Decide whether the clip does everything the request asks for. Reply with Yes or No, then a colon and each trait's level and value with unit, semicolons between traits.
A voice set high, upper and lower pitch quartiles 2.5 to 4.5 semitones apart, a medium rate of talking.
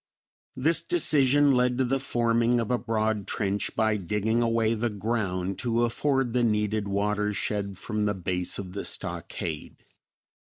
No: low, 110 Hz; average, 2.9 semitones; average, 150 wpm